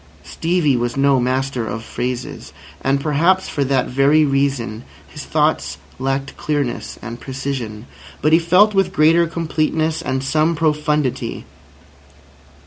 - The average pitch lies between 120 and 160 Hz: Yes, medium, 140 Hz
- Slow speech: Yes, slow, 130 wpm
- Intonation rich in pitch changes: No, average, 3.4 semitones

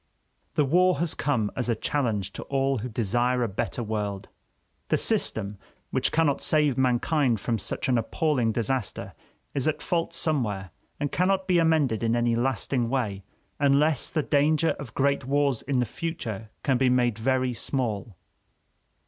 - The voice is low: Yes, low, 130 Hz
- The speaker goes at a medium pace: Yes, average, 160 wpm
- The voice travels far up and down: No, average, 4.2 semitones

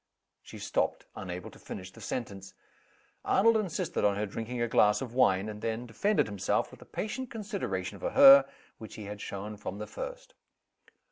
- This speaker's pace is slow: No, average, 180 wpm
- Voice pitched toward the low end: Yes, low, 110 Hz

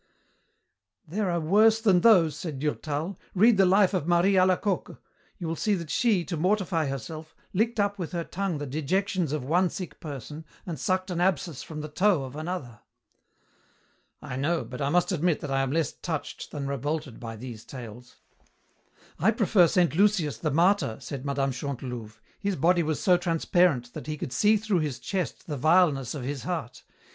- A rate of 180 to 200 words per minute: Yes, average, 185 wpm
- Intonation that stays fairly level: No, average, 4.9 semitones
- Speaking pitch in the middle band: Yes, medium, 165 Hz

